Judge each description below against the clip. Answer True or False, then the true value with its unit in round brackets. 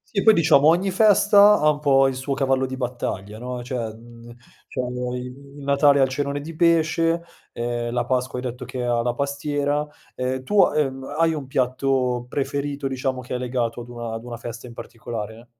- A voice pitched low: True (130 Hz)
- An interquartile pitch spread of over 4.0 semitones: False (2.9 semitones)